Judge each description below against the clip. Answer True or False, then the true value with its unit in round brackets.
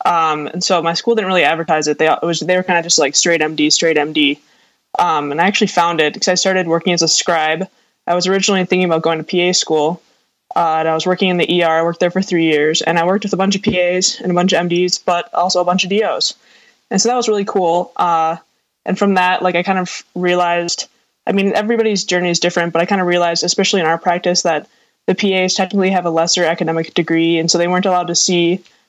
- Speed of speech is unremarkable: False (255 wpm)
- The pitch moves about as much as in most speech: False (2.1 semitones)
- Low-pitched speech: False (175 Hz)